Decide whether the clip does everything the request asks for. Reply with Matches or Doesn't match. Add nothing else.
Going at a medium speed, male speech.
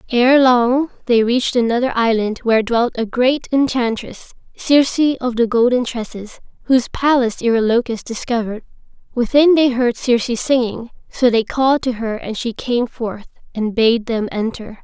Doesn't match